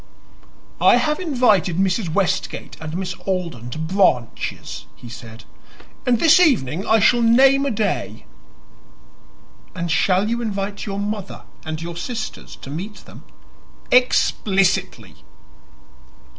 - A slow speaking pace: Yes, slow, 120 wpm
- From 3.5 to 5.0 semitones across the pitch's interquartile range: No, wide, 5.5 semitones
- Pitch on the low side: No, high, 195 Hz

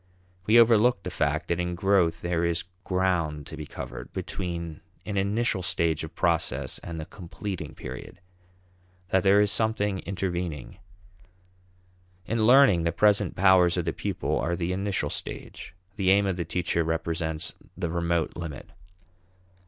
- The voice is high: No, very low, 90 Hz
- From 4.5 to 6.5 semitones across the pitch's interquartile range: No, average, 3.0 semitones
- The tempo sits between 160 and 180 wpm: No, average, 150 wpm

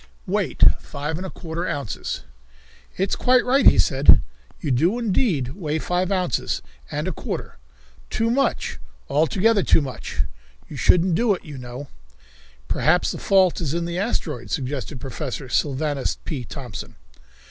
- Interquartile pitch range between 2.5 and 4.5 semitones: No, wide, 5.6 semitones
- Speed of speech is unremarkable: Yes, average, 155 wpm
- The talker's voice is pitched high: No, medium, 160 Hz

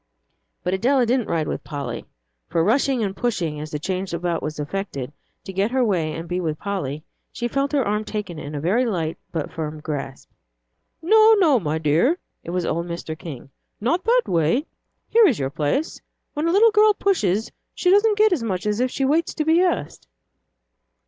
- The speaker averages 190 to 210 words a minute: Yes, average, 195 wpm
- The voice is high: Yes, high, 200 Hz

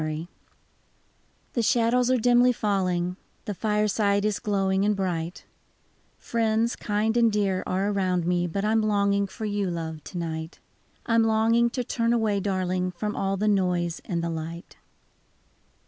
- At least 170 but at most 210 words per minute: No, average, 160 wpm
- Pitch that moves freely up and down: No, average, 3.5 semitones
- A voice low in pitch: No, high, 200 Hz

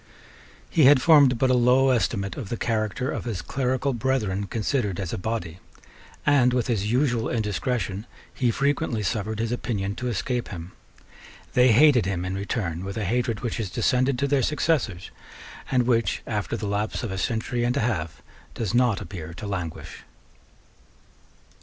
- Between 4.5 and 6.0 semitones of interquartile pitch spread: No, average, 4.1 semitones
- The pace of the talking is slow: No, average, 170 wpm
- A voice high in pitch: No, low, 115 Hz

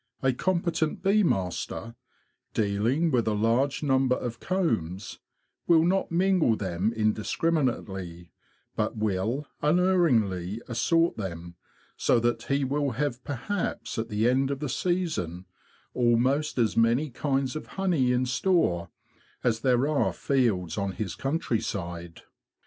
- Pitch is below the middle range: Yes, low, 125 Hz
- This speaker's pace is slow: Yes, slow, 125 wpm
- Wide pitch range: Yes, wide, 6.2 semitones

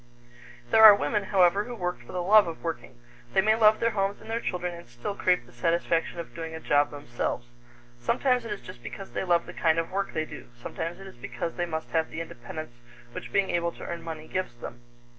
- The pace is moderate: No, fast, 235 wpm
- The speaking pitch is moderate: Yes, medium, 170 Hz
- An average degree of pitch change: Yes, average, 3.9 semitones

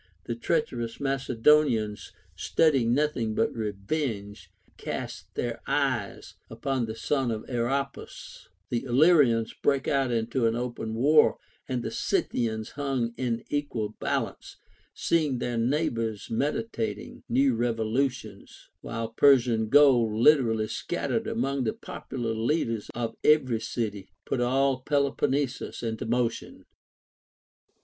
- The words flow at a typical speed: No, slow, 120 wpm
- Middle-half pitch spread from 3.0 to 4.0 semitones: Yes, average, 3.5 semitones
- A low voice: Yes, low, 120 Hz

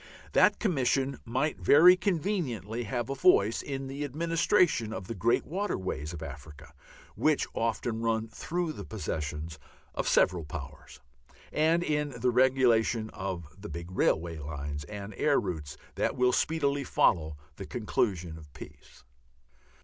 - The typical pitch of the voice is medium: No, low, 115 Hz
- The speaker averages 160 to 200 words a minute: No, average, 140 wpm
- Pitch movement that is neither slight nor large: No, wide, 8.8 semitones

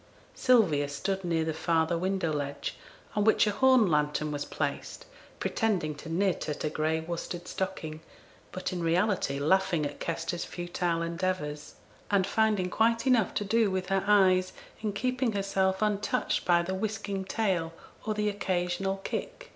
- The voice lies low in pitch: No, medium, 185 Hz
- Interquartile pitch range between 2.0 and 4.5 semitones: Yes, average, 3.9 semitones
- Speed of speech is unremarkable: Yes, average, 155 wpm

